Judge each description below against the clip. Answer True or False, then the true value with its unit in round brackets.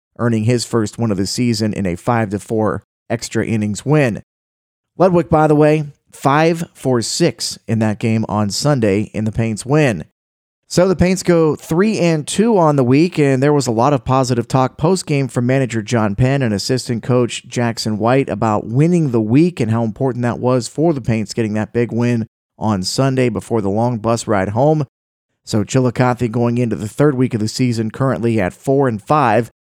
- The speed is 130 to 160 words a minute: False (195 wpm)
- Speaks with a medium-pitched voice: False (120 Hz)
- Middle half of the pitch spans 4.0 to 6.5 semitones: True (4.3 semitones)